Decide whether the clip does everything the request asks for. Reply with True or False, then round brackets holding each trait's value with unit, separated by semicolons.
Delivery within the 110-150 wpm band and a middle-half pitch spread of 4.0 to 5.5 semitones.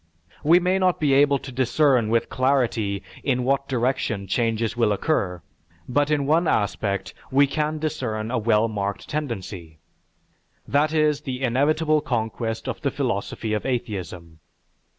True (145 wpm; 5.2 semitones)